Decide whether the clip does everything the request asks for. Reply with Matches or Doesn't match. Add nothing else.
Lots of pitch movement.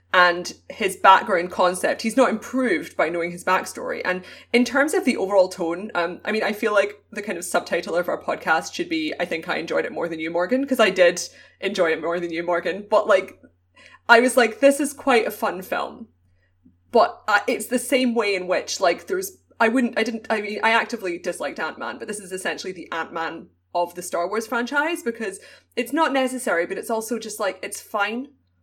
Matches